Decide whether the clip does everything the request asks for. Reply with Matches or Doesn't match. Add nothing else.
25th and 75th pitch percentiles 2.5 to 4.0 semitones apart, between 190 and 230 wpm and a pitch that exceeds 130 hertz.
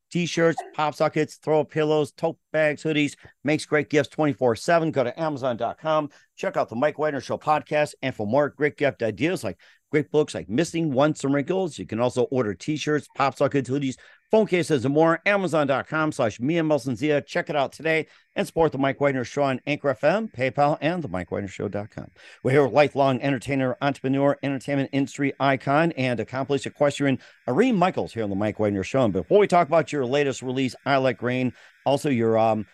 Matches